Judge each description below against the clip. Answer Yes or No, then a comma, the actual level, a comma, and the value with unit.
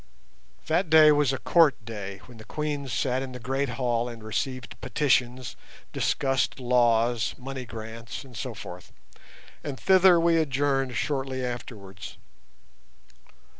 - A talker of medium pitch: No, low, 130 Hz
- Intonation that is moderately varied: Yes, average, 3.4 semitones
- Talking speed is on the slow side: Yes, slow, 130 wpm